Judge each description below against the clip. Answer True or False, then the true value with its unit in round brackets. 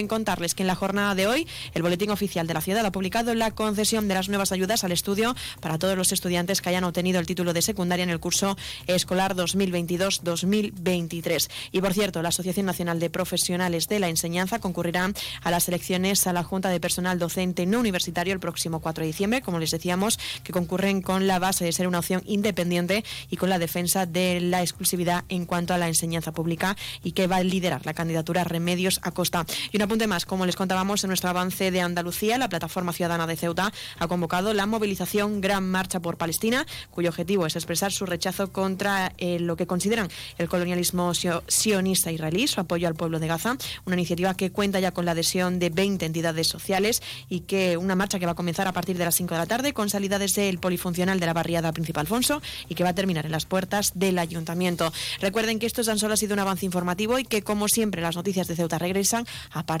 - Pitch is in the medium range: True (180 Hz)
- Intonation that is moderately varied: False (2.2 semitones)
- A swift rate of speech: True (220 wpm)